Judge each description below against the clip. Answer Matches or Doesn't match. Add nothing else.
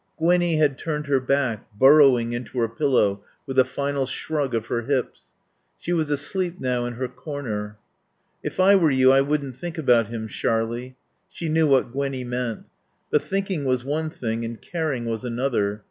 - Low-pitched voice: Matches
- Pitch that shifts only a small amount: Doesn't match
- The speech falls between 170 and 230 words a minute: Matches